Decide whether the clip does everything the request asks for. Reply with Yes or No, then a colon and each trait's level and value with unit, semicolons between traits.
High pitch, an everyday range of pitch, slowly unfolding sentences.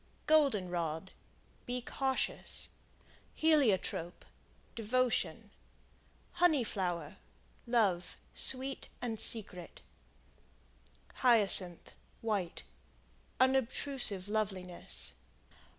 No: high, 220 Hz; wide, 6.1 semitones; slow, 60 wpm